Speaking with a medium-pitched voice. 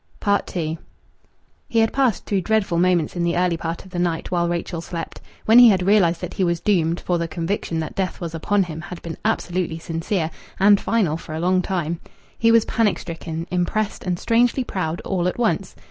Yes: medium, 180 Hz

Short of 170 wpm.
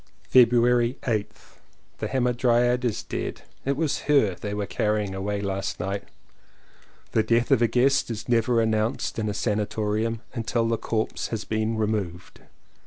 Yes: average, 150 wpm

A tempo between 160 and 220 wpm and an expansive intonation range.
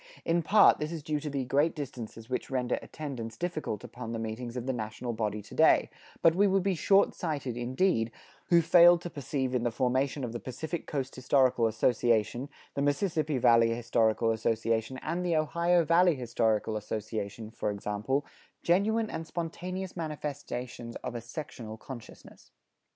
Yes: average, 165 wpm; wide, 5.9 semitones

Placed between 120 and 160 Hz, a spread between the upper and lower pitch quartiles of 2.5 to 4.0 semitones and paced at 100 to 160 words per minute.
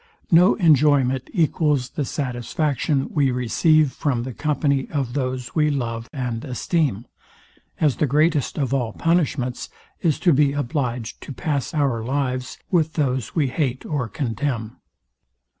Yes: medium, 140 Hz; average, 3.4 semitones; average, 140 wpm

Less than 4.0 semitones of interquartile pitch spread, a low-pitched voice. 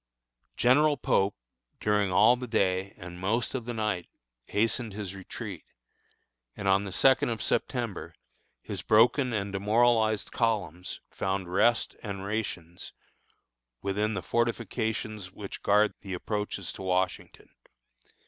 Yes: average, 3.0 semitones; low, 105 Hz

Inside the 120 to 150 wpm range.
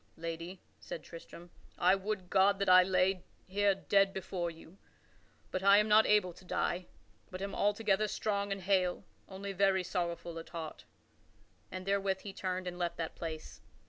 No: average, 170 wpm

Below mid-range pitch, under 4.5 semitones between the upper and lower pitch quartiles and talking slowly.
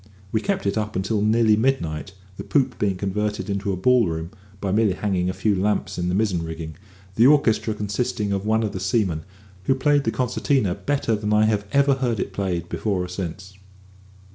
No: low, 105 Hz; average, 3.3 semitones; average, 195 wpm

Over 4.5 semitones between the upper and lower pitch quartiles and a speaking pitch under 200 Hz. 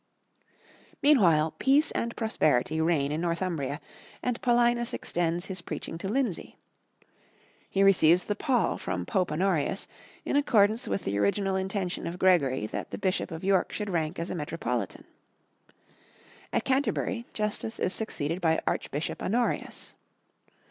Yes: wide, 5.4 semitones; medium, 185 Hz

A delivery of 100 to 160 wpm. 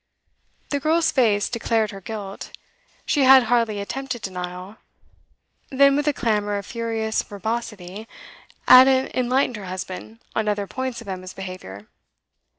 Yes: slow, 135 wpm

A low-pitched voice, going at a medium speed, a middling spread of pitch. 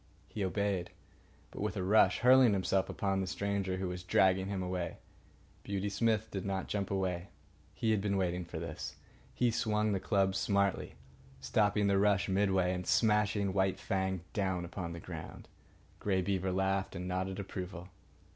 No: very low, 95 Hz; average, 165 wpm; narrow, 1.5 semitones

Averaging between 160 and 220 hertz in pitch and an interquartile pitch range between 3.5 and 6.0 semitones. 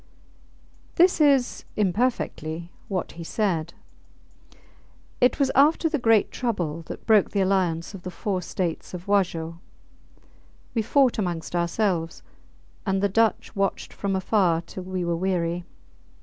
Yes: high, 190 Hz; average, 4.3 semitones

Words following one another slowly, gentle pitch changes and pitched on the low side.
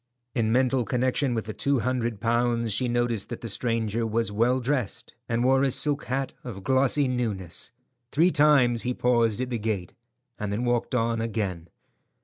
No: average, 175 wpm; narrow, 2.3 semitones; low, 120 Hz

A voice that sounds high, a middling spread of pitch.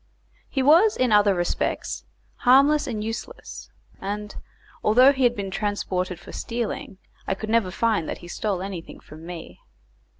Yes: high, 210 Hz; average, 4.6 semitones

